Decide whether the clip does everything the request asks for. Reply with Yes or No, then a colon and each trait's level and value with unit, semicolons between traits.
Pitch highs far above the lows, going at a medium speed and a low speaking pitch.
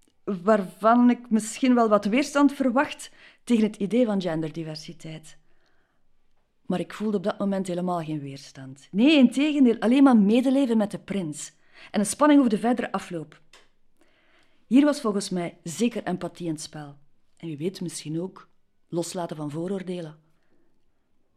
No: wide, 6.3 semitones; average, 150 wpm; high, 195 Hz